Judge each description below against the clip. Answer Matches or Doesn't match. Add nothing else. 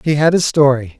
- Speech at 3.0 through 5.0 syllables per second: Doesn't match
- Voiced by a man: Matches